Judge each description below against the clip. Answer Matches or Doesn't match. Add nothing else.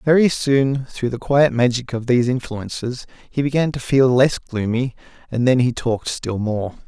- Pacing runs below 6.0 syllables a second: Matches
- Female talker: Doesn't match